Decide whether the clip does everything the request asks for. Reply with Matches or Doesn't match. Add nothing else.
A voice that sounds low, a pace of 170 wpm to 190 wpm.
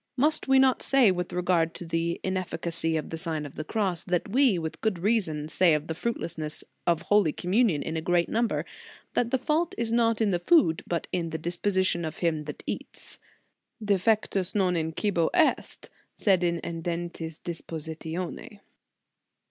Doesn't match